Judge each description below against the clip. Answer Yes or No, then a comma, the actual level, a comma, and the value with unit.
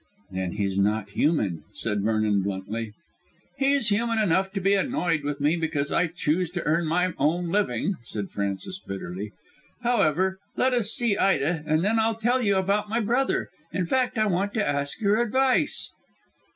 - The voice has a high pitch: No, medium, 175 Hz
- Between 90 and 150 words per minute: No, average, 175 wpm